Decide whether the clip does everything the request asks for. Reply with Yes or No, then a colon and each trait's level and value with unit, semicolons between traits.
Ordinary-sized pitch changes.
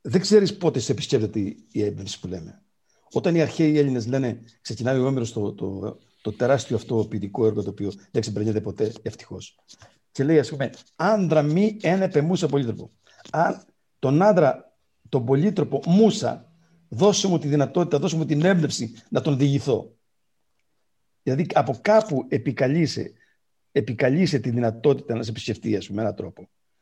No: wide, 6.3 semitones